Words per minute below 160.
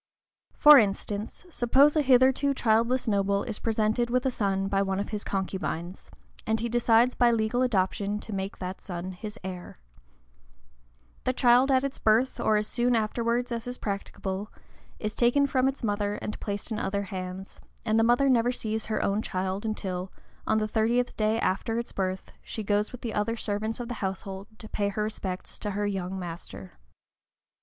No: average, 180 wpm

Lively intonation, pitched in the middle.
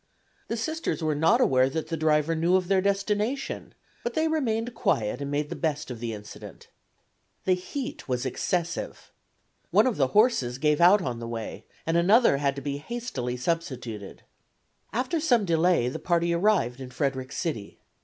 Yes: wide, 7.7 semitones; medium, 165 Hz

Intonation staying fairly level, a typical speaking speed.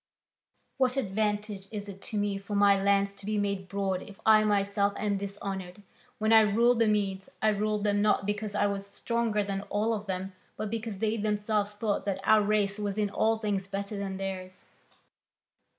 Yes: narrow, 1.4 semitones; average, 190 wpm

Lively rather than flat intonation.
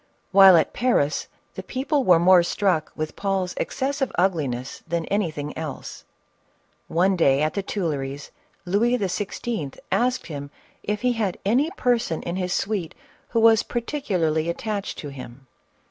Yes: wide, 6.0 semitones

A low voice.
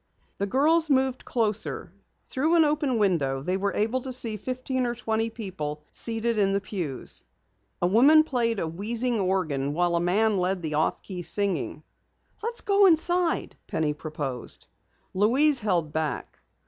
No: high, 210 Hz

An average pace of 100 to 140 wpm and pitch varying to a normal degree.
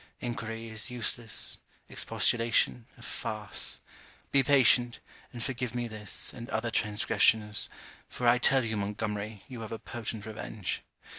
No: slow, 135 wpm; narrow, 2.0 semitones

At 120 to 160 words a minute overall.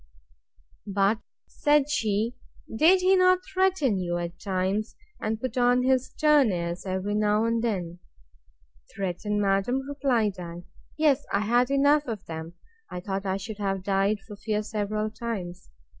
Yes: average, 145 wpm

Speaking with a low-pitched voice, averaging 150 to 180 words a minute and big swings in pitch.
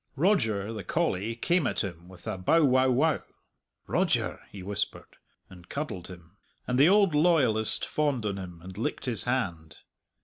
Yes: low, 110 Hz; average, 165 wpm; wide, 7.4 semitones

